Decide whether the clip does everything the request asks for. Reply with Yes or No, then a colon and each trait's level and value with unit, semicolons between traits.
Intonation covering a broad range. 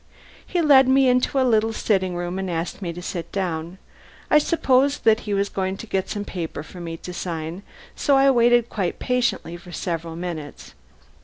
Yes: wide, 6.3 semitones